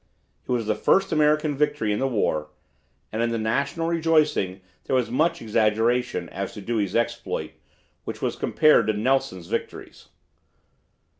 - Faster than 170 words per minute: No, average, 150 wpm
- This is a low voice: Yes, low, 115 Hz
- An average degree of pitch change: No, wide, 5.9 semitones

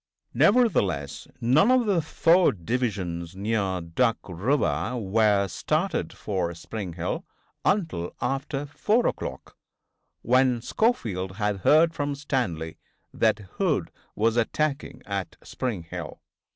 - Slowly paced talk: Yes, slow, 110 wpm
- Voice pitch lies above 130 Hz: No, low, 115 Hz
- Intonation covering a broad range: Yes, wide, 7.8 semitones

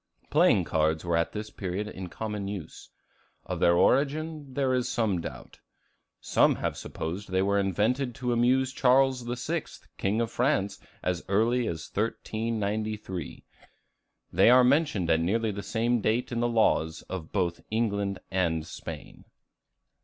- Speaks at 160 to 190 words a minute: No, average, 145 wpm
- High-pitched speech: No, low, 110 Hz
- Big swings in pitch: No, average, 4.8 semitones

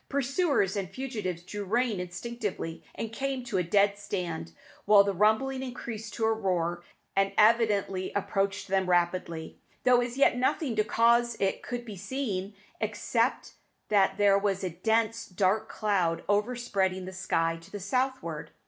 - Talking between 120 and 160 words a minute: Yes, average, 155 wpm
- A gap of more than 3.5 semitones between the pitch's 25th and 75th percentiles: Yes, average, 4.1 semitones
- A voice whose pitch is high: Yes, high, 205 Hz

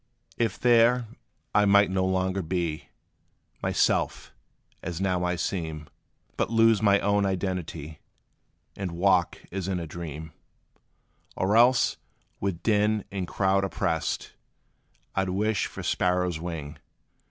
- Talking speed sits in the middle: No, slow, 125 wpm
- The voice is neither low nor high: No, very low, 95 Hz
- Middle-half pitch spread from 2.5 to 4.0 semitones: Yes, average, 2.9 semitones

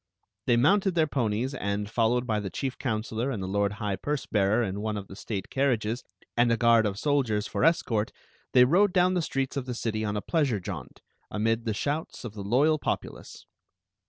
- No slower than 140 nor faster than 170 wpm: No, fast, 205 wpm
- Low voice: Yes, low, 115 Hz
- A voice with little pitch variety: No, average, 4.7 semitones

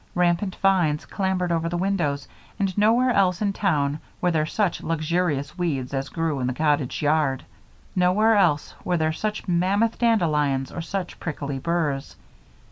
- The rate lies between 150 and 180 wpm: Yes, average, 155 wpm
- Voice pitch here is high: No, medium, 170 Hz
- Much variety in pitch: No, average, 4.5 semitones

